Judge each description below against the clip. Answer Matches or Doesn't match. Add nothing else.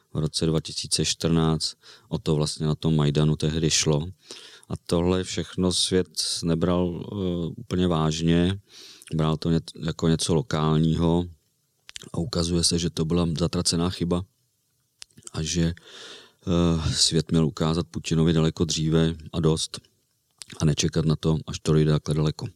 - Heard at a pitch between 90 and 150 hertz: Doesn't match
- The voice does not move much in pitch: Matches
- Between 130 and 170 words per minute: Matches